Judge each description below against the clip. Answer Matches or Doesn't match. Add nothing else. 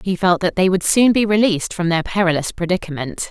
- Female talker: Matches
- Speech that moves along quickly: Matches